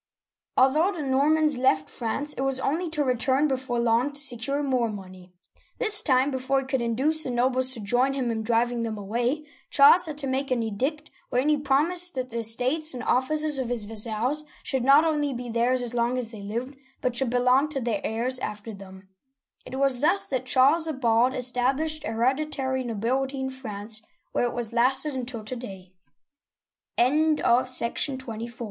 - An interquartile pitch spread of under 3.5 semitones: Yes, average, 3.1 semitones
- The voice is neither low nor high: No, very high, 255 Hz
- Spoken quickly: No, average, 180 wpm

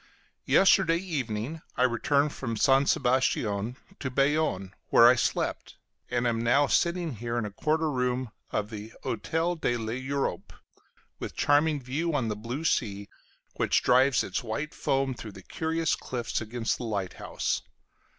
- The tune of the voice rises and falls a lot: No, average, 4.5 semitones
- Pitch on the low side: Yes, low, 125 Hz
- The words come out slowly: No, average, 150 wpm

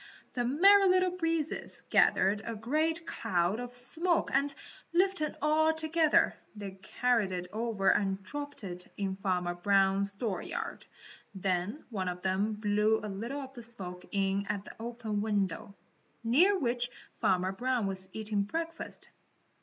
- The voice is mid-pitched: No, high, 220 Hz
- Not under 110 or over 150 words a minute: Yes, average, 145 wpm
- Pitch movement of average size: No, wide, 6.9 semitones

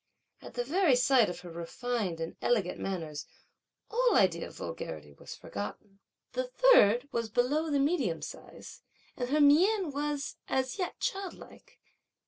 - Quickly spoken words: No, average, 145 wpm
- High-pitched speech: Yes, very high, 250 Hz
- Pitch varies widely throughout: Yes, wide, 8.9 semitones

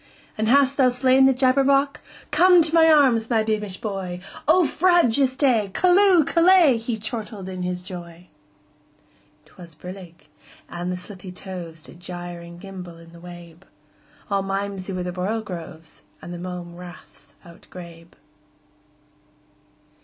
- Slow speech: Yes, slow, 120 wpm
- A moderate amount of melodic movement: No, wide, 6.9 semitones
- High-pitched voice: Yes, high, 195 Hz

